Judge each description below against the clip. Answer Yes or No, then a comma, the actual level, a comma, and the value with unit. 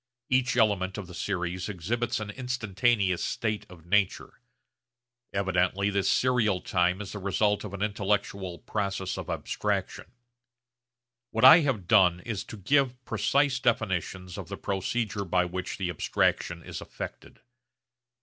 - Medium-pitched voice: No, low, 100 Hz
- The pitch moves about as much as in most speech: Yes, average, 3.4 semitones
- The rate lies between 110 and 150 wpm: Yes, average, 140 wpm